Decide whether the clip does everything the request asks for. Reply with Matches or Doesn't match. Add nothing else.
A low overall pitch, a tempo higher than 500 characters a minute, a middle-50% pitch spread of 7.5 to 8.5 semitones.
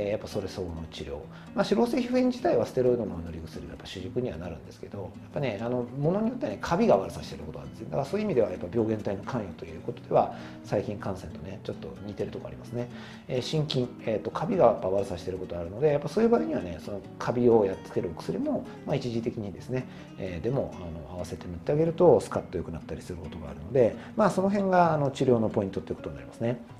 Matches